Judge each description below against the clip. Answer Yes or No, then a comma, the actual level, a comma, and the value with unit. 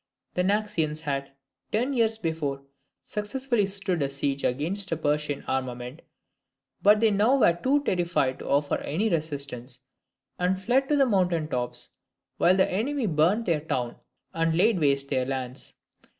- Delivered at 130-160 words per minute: Yes, average, 150 wpm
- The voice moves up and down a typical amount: No, wide, 6.8 semitones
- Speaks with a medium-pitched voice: Yes, medium, 170 Hz